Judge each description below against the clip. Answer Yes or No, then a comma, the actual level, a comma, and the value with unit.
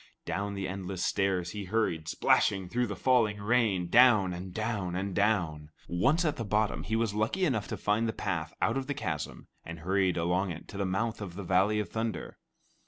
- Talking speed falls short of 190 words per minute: No, fast, 205 wpm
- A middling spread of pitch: Yes, average, 3.5 semitones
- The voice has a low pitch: Yes, low, 100 Hz